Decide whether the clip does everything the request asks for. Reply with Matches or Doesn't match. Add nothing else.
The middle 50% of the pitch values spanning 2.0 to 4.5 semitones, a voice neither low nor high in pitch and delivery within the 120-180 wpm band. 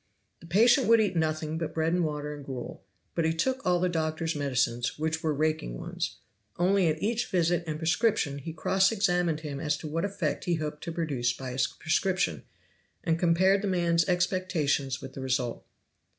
Doesn't match